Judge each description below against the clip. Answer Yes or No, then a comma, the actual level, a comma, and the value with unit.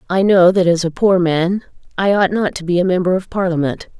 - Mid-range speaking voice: Yes, medium, 180 Hz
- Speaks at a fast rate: Yes, fast, 240 wpm